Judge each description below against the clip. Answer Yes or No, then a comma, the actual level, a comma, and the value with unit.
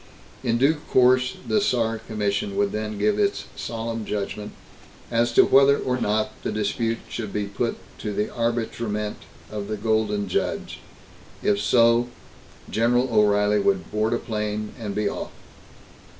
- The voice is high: No, low, 110 Hz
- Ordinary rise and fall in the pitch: No, narrow, 2.3 semitones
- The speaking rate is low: No, average, 150 wpm